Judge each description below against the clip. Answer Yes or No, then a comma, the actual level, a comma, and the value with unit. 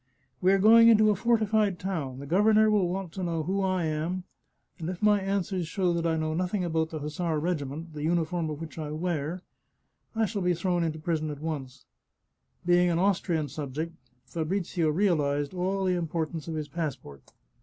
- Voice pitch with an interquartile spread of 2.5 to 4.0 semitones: Yes, average, 3.4 semitones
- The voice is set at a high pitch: No, medium, 170 Hz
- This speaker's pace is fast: No, average, 195 wpm